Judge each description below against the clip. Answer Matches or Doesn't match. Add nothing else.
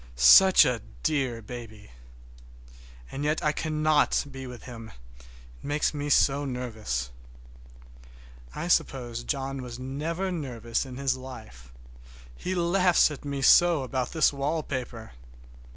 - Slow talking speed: Matches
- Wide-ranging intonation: Doesn't match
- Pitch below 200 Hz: Matches